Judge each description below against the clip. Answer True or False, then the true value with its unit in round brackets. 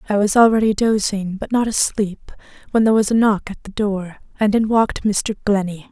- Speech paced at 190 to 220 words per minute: True (205 wpm)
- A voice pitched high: True (210 Hz)